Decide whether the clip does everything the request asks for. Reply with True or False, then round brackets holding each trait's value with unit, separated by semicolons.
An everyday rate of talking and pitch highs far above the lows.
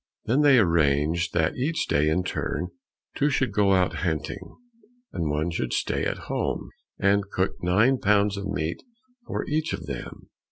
False (165 wpm; 4.6 semitones)